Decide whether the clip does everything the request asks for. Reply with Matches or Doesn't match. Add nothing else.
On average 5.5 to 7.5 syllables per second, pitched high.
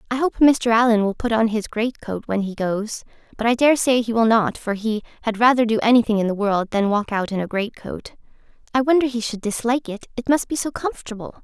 Matches